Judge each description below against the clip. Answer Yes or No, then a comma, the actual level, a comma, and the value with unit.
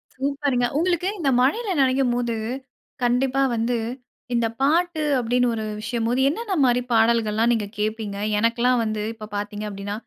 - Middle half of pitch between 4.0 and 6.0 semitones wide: No, average, 3.5 semitones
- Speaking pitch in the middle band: No, high, 240 Hz